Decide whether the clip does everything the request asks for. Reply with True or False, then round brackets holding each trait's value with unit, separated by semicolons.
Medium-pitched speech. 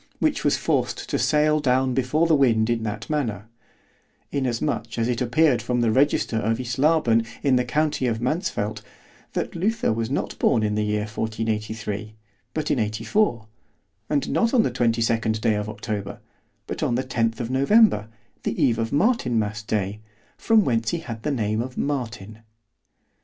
False (120 Hz)